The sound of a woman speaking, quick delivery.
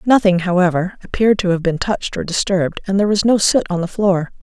Yes: female; fast, 225 wpm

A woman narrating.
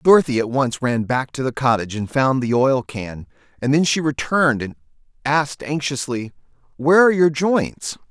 No: male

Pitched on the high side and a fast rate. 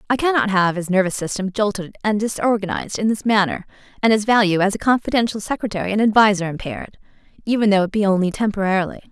No: high, 205 Hz; average, 185 wpm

